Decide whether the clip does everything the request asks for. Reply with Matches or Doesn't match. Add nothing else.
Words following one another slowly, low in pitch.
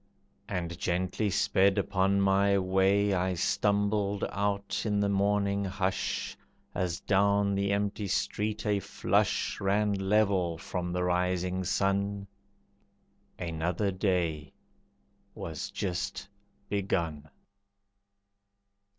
Matches